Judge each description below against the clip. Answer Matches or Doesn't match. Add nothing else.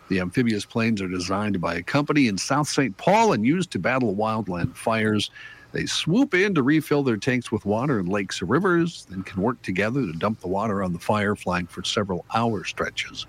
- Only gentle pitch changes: Doesn't match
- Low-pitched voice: Matches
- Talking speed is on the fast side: Matches